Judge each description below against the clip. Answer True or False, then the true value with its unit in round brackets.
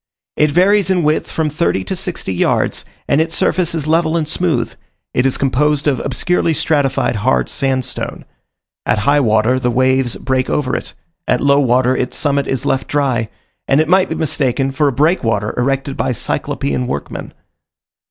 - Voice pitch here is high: False (140 Hz)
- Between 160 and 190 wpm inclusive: True (175 wpm)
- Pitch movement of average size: True (3.8 semitones)